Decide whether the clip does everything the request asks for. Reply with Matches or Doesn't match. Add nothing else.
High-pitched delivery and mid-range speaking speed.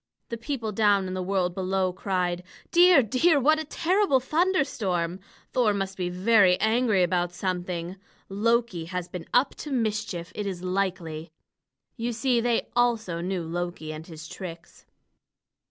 Matches